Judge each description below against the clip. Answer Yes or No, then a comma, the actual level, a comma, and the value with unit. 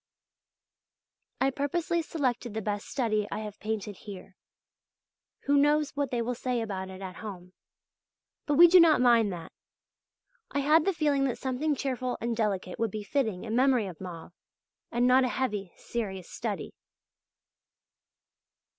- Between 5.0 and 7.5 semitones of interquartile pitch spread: Yes, average, 5.3 semitones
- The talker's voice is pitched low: No, high, 235 Hz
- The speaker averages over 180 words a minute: No, average, 155 wpm